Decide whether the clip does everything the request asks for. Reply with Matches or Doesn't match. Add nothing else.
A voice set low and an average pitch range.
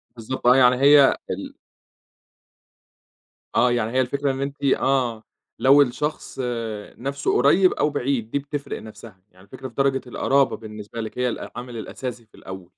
Matches